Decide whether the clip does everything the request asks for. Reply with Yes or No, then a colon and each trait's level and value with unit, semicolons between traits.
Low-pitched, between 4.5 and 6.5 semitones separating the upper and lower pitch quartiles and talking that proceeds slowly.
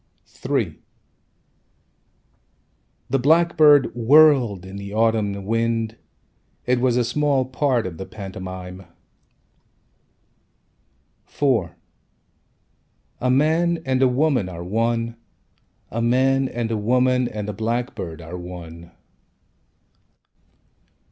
Yes: low, 115 Hz; average, 4.8 semitones; slow, 95 wpm